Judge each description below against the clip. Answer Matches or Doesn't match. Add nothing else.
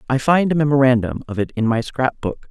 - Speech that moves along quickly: Matches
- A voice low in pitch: Matches